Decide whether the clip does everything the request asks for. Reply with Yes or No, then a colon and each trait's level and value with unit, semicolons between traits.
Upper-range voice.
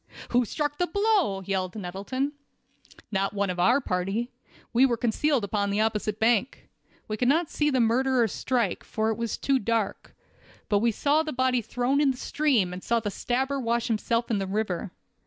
Yes: high, 235 Hz